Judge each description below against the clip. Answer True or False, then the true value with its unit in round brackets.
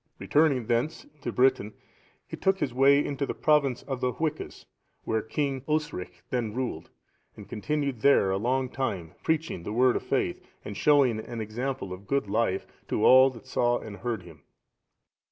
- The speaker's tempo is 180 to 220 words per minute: False (170 wpm)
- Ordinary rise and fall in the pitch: True (4.3 semitones)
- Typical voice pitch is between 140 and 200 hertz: False (125 Hz)